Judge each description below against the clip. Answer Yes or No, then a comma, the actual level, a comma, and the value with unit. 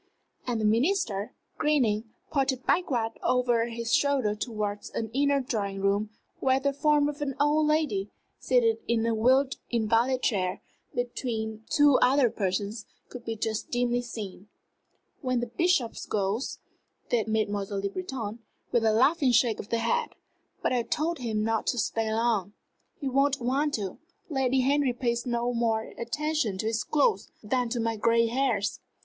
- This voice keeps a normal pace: Yes, average, 160 wpm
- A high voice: Yes, high, 235 Hz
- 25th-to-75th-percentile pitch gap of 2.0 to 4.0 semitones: Yes, average, 3.5 semitones